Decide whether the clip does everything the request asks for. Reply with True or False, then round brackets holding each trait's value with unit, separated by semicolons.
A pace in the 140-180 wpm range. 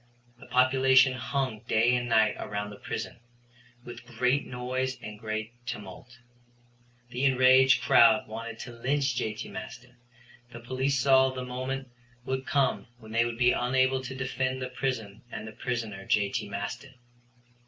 True (150 wpm)